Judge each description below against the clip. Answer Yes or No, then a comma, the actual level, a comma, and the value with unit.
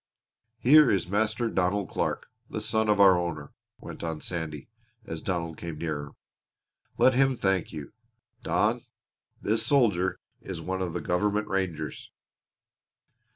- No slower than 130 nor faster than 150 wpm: Yes, slow, 135 wpm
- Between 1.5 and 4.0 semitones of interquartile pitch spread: No, average, 4.4 semitones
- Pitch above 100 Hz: No, very low, 95 Hz